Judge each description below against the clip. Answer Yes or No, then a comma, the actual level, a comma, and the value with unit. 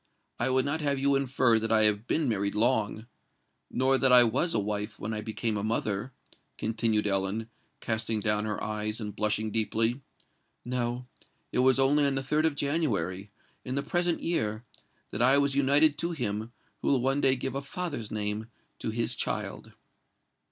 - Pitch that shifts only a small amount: No, average, 4.2 semitones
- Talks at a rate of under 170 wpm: No, average, 175 wpm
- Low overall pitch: Yes, low, 120 Hz